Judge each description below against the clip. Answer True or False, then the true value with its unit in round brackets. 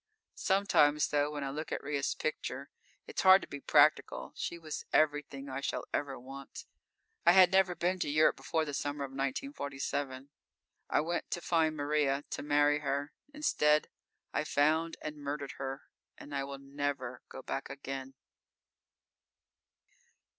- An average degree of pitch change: False (2.1 semitones)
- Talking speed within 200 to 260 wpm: False (155 wpm)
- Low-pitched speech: False (145 Hz)